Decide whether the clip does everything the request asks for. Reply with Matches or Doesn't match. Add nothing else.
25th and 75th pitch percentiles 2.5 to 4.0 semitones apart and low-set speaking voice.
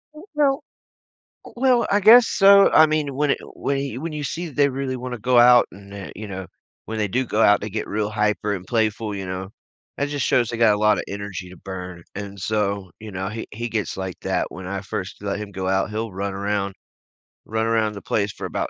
Doesn't match